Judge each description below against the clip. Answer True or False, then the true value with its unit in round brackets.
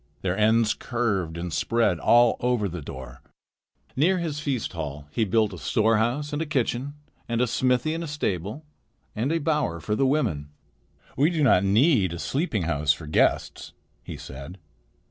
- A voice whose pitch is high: False (115 Hz)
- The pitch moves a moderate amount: False (8.0 semitones)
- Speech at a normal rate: True (170 wpm)